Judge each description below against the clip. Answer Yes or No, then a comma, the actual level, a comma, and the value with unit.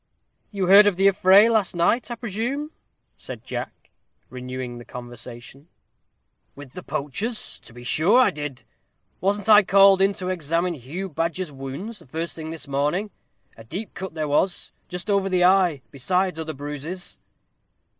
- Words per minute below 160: No, average, 165 wpm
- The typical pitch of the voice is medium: Yes, medium, 175 Hz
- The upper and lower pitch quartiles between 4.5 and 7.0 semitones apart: Yes, wide, 5.4 semitones